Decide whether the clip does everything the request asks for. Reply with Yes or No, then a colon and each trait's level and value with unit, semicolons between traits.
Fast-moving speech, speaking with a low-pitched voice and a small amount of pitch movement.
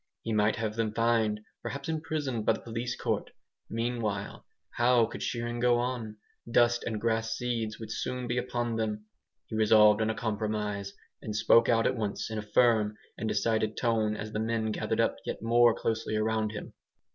No: average, 180 wpm; low, 110 Hz; narrow, 1.8 semitones